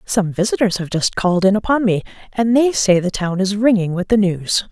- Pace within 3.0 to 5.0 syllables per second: No, 5.3 syllables/s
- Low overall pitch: No, high, 200 Hz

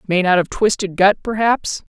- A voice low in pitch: No, high, 200 Hz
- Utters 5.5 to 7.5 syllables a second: No, 4.7 syllables/s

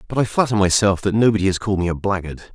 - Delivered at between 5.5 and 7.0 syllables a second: No, 7.5 syllables/s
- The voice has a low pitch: Yes, low, 100 Hz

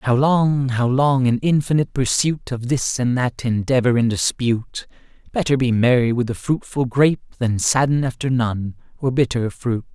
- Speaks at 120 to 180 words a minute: Yes, average, 170 wpm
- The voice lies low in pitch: Yes, low, 125 Hz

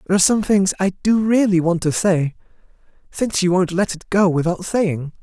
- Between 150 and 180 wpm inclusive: No, fast, 205 wpm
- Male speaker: Yes, male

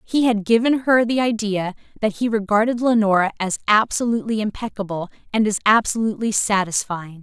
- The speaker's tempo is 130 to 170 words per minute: Yes, average, 140 wpm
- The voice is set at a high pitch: Yes, high, 215 Hz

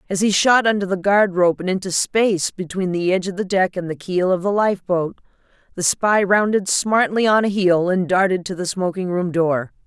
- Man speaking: No, female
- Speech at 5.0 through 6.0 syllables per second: Yes, 5.3 syllables/s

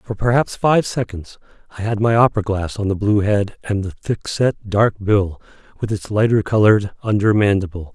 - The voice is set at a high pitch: No, low, 105 Hz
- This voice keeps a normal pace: Yes, average, 190 wpm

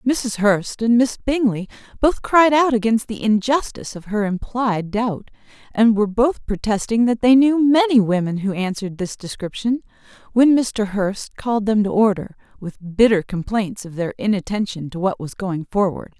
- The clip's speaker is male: No, female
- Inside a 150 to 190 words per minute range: Yes, average, 170 wpm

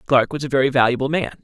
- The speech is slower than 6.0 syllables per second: No, 7.0 syllables/s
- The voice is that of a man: Yes, male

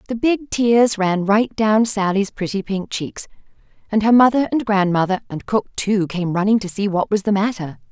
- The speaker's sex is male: No, female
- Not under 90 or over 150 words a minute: No, average, 195 wpm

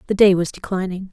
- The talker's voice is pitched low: No, high, 190 Hz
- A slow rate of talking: No, fast, 215 wpm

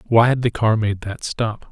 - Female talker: No, male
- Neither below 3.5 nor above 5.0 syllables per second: Yes, 4.7 syllables/s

